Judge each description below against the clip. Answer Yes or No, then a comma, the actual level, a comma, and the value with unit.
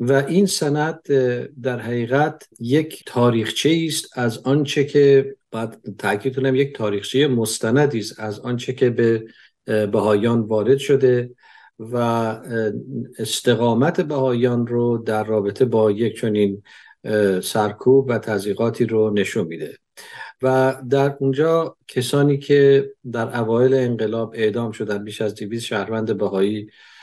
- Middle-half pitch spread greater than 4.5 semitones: No, average, 3.6 semitones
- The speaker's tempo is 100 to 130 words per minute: Yes, average, 120 wpm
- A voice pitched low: Yes, low, 120 Hz